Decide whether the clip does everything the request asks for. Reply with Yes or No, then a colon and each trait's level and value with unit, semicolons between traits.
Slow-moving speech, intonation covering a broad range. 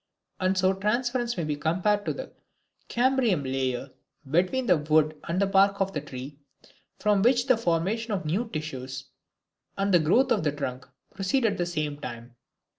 No: average, 175 wpm; wide, 6.2 semitones